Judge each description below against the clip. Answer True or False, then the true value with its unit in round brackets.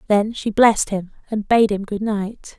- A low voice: False (210 Hz)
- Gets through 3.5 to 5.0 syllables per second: True (4.5 syllables/s)